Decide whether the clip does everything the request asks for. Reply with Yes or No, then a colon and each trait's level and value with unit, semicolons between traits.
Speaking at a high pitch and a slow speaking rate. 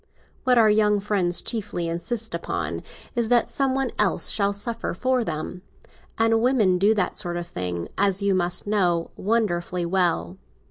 No: high, 200 Hz; average, 165 wpm